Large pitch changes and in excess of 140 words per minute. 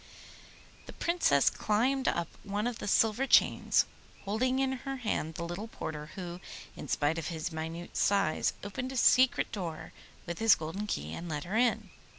Yes: wide, 6.9 semitones; average, 170 wpm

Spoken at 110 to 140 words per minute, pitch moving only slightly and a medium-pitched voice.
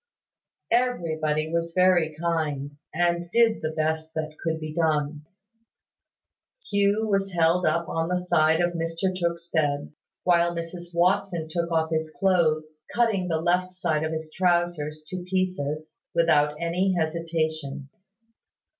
Yes: slow, 135 wpm; narrow, 2.3 semitones; medium, 165 Hz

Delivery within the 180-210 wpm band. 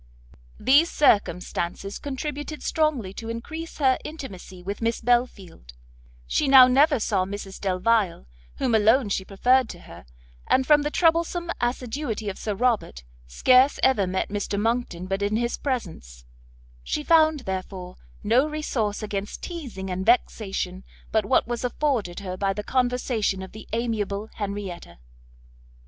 No: average, 140 wpm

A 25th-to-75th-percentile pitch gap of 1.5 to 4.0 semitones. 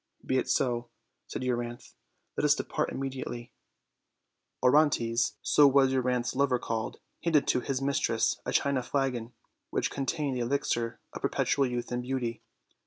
Yes: narrow, 2.4 semitones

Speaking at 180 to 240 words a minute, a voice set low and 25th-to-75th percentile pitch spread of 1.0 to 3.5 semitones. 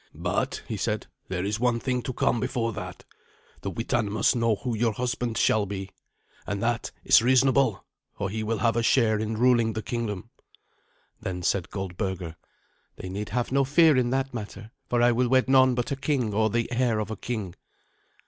Yes: average, 195 wpm; low, 115 Hz; average, 3.2 semitones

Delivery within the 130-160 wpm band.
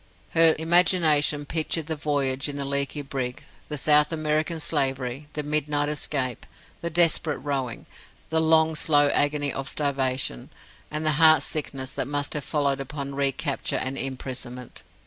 Yes: average, 145 wpm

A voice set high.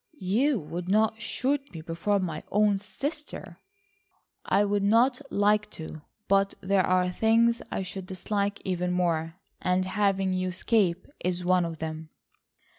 Yes: high, 195 Hz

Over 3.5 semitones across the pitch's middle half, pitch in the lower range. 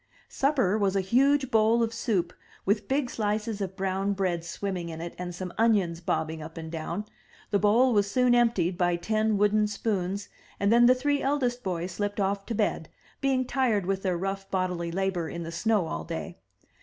No: average, 4.2 semitones; high, 200 Hz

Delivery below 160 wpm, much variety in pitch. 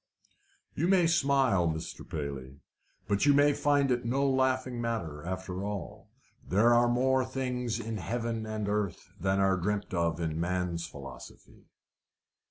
Yes: average, 145 wpm; wide, 6.3 semitones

